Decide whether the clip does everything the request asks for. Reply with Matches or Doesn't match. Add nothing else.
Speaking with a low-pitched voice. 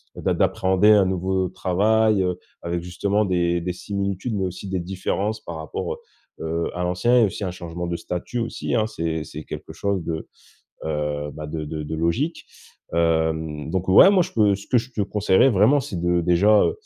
Matches